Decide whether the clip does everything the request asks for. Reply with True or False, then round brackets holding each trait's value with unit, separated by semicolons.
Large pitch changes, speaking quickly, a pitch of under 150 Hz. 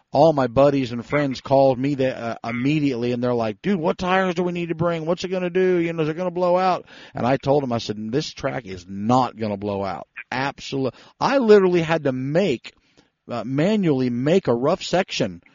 True (6.4 semitones; 230 wpm; 140 Hz)